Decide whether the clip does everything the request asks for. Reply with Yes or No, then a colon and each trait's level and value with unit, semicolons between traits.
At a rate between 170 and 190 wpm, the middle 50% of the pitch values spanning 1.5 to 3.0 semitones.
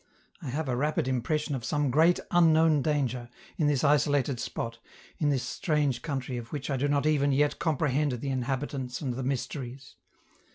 Yes: average, 175 wpm; average, 2.7 semitones